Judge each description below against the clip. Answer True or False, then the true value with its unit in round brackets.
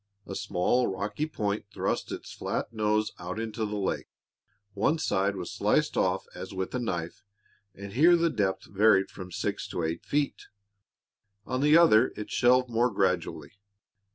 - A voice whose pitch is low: True (105 Hz)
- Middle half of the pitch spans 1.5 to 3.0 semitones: False (4.8 semitones)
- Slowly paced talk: False (160 wpm)